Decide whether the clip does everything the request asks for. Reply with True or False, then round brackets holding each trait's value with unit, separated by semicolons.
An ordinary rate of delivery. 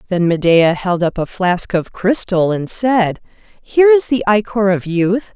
True (180 wpm)